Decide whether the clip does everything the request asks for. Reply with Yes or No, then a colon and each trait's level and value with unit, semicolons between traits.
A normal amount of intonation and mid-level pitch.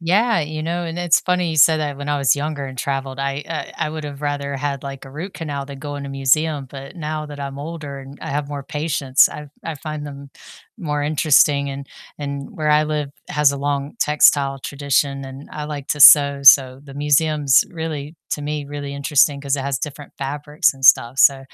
No: narrow, 1.6 semitones; medium, 145 Hz